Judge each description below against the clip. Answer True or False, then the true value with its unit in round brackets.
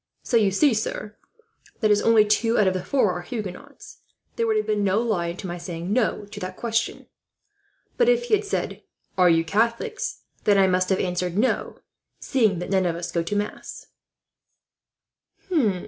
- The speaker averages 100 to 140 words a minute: False (180 wpm)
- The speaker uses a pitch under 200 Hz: False (205 Hz)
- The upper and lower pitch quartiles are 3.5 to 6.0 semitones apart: True (4.2 semitones)